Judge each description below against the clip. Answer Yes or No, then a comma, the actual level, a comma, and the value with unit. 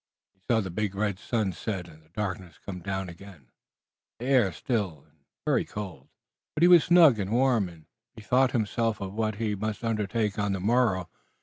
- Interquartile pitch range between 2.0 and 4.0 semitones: Yes, average, 3.5 semitones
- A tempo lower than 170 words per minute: No, average, 190 wpm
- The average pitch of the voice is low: Yes, low, 105 Hz